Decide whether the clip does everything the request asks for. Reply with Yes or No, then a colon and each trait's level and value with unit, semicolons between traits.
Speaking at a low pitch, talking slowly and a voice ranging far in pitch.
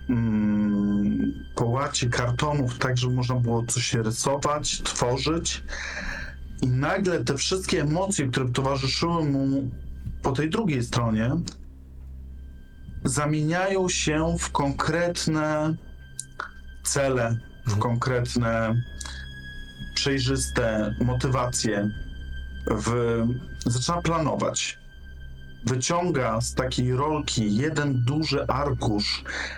Yes: low, 125 Hz; slow, 80 wpm; wide, 5.8 semitones